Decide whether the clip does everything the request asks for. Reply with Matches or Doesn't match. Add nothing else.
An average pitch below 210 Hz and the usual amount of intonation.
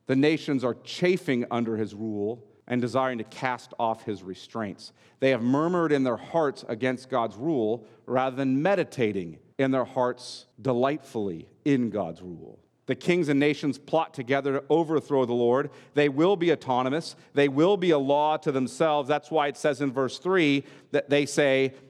Matches